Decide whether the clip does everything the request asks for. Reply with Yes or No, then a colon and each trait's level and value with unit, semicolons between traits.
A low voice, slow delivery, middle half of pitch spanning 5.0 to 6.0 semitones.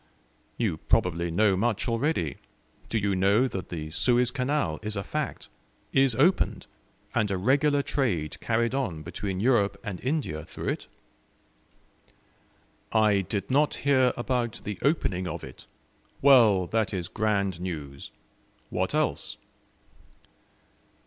Yes: low, 110 Hz; slow, 130 wpm; wide, 5.6 semitones